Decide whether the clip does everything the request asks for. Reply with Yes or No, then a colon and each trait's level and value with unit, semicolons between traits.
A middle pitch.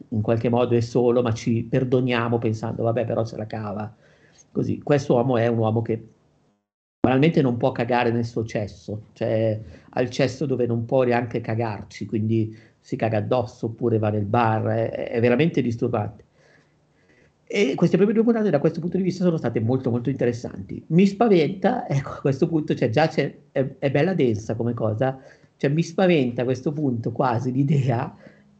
No: low, 120 Hz